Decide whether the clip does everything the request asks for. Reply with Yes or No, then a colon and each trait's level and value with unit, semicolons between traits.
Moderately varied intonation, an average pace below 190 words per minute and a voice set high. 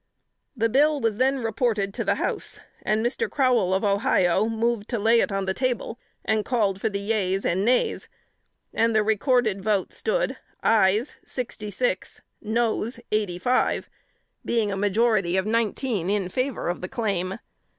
Yes: average, 3.3 semitones; average, 160 wpm; high, 220 Hz